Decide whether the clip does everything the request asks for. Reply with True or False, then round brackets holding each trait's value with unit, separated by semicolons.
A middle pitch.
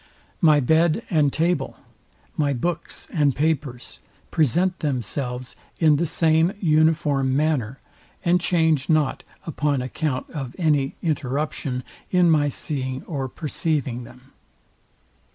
True (150 Hz)